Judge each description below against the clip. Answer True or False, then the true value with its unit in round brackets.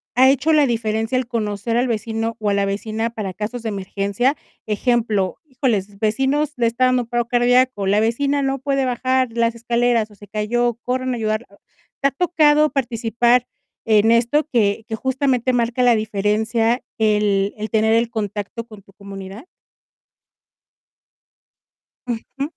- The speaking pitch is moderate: False (230 Hz)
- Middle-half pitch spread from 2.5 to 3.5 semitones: True (3.0 semitones)